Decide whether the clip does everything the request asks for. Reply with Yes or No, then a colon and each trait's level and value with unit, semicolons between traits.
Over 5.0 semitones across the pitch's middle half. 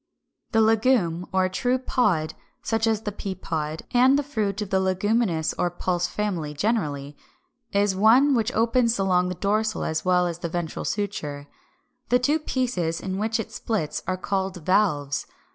No: average, 4.3 semitones